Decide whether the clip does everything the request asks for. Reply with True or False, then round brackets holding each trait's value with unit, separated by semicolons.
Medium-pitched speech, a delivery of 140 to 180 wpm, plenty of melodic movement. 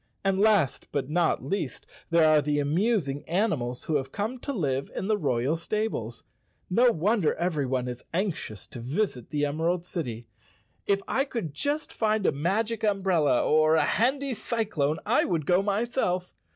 True (175 Hz; 165 wpm; 6.7 semitones)